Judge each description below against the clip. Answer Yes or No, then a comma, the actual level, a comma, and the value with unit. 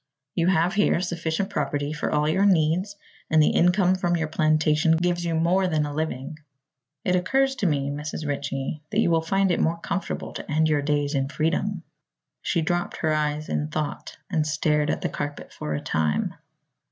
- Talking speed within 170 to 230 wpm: Yes, average, 190 wpm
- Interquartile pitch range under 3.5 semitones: Yes, average, 2.9 semitones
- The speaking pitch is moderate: Yes, medium, 160 Hz